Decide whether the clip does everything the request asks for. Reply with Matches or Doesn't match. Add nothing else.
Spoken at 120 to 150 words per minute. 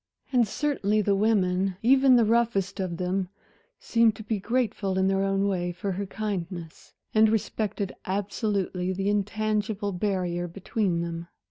Matches